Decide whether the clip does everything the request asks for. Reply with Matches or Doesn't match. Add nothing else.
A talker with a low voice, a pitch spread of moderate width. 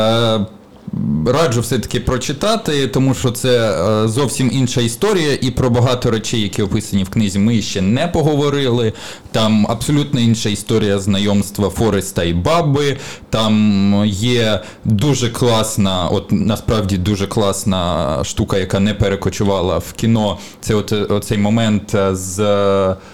Matches